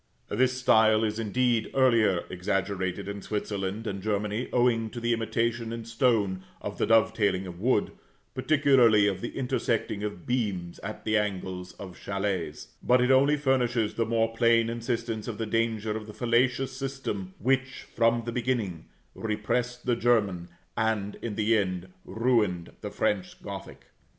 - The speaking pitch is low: Yes, low, 110 Hz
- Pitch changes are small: No, average, 3.1 semitones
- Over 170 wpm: No, average, 155 wpm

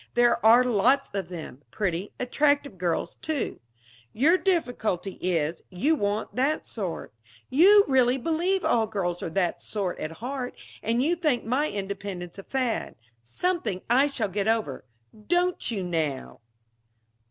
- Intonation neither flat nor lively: No, wide, 7.2 semitones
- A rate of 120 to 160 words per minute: Yes, average, 140 wpm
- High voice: Yes, high, 225 Hz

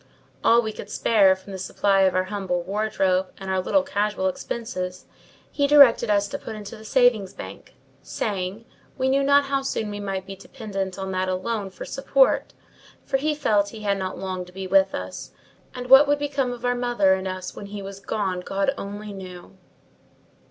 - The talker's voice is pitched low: No, high, 205 Hz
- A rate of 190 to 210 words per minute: Yes, average, 195 wpm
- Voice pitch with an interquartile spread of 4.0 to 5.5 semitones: Yes, average, 4.4 semitones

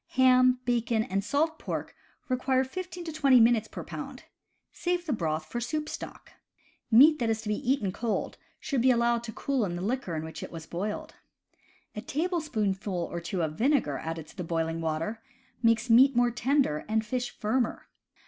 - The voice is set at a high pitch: Yes, high, 235 Hz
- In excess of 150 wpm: Yes, average, 185 wpm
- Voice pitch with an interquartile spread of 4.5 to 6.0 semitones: Yes, wide, 5.5 semitones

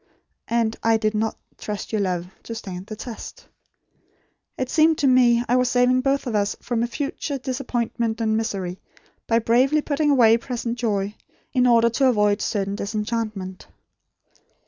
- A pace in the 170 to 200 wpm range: No, average, 155 wpm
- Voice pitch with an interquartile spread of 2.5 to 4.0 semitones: Yes, average, 3.0 semitones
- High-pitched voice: Yes, high, 230 Hz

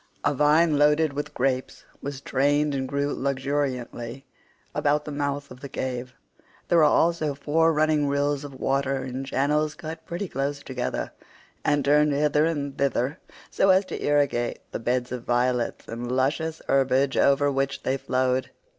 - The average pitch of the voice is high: No, medium, 140 Hz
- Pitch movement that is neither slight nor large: No, narrow, 2.2 semitones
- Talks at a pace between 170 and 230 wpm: No, average, 160 wpm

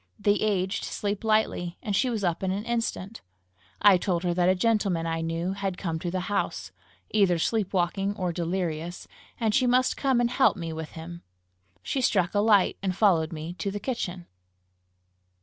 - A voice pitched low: No, high, 190 Hz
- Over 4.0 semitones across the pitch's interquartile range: No, average, 3.4 semitones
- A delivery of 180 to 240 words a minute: Yes, average, 185 wpm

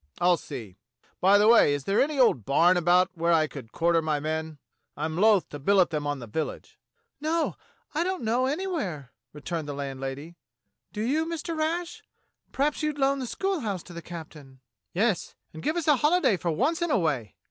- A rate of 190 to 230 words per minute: Yes, average, 195 wpm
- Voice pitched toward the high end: No, medium, 180 Hz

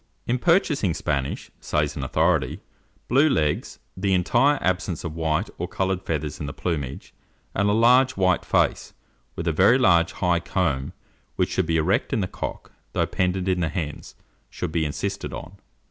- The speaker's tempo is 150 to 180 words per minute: Yes, average, 175 wpm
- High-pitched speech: No, very low, 90 Hz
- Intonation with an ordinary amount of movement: Yes, average, 4.1 semitones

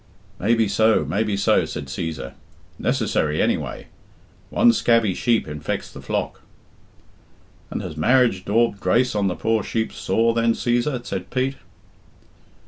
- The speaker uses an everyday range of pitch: Yes, average, 3.4 semitones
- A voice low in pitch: Yes, low, 115 Hz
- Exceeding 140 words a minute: No, slow, 135 wpm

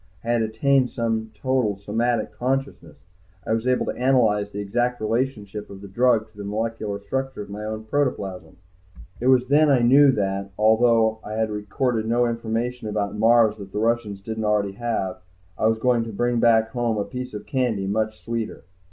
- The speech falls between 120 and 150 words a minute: No, average, 185 wpm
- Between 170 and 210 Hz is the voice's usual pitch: No, low, 110 Hz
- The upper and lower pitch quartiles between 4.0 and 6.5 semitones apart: No, average, 2.7 semitones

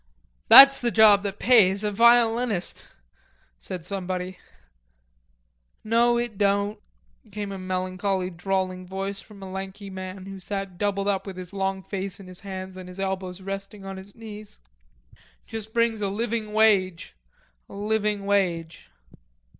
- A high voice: Yes, high, 195 Hz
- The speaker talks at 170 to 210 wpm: No, average, 145 wpm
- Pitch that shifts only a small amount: Yes, narrow, 2.1 semitones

